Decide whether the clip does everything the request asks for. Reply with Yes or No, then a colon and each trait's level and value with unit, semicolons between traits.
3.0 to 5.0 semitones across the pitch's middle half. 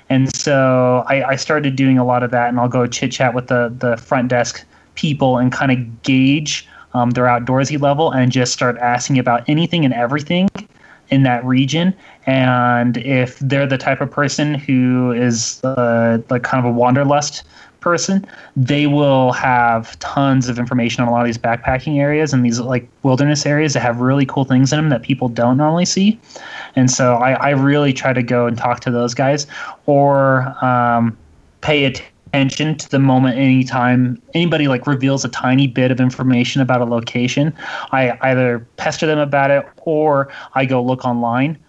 No: narrow, 2.4 semitones